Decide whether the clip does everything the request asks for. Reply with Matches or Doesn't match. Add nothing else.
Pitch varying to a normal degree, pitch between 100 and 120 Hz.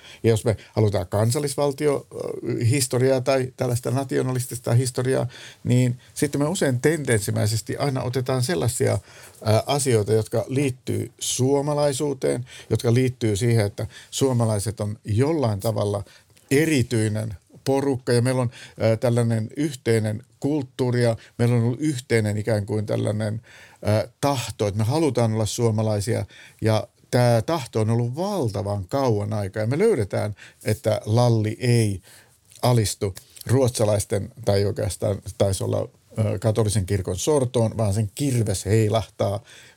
Matches